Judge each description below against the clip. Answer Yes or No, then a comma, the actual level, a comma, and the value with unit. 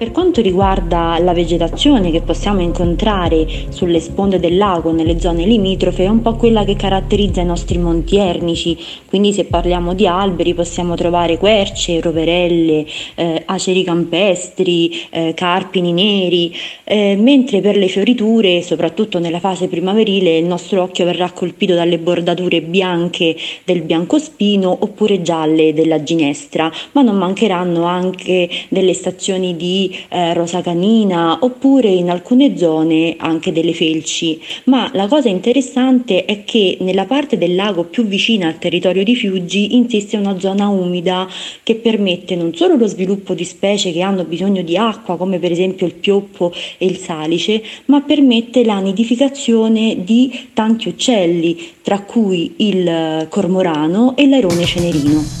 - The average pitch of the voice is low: No, medium, 185 Hz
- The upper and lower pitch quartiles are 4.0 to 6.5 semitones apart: No, average, 3.2 semitones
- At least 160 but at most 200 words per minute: No, average, 145 wpm